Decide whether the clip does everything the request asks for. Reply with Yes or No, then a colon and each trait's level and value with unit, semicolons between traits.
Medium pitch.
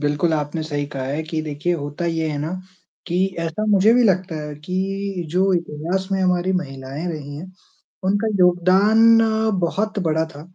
Yes: medium, 175 Hz